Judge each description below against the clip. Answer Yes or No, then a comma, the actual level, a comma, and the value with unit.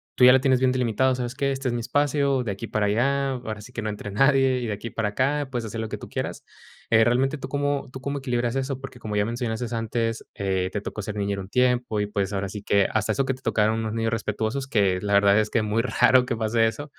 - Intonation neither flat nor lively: Yes, average, 3.7 semitones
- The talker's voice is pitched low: Yes, low, 115 Hz